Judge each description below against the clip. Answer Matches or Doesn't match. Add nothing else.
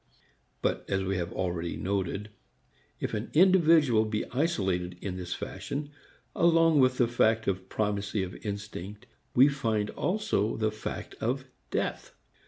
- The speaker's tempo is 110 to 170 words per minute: Matches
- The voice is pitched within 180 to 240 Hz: Doesn't match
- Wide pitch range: Matches